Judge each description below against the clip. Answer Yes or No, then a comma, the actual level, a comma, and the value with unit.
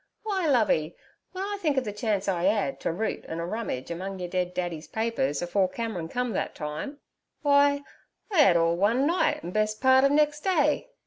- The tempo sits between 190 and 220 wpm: Yes, average, 195 wpm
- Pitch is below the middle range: No, high, 215 Hz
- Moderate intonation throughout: No, wide, 8.2 semitones